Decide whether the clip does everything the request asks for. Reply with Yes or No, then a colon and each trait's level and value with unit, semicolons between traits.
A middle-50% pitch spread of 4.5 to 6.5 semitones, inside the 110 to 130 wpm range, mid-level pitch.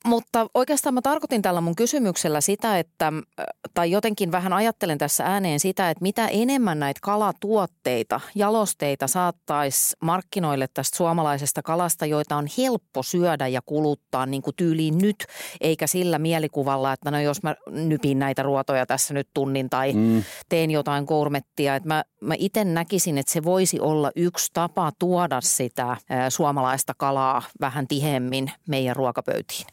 No: average, 5.0 semitones; average, 145 wpm; medium, 155 Hz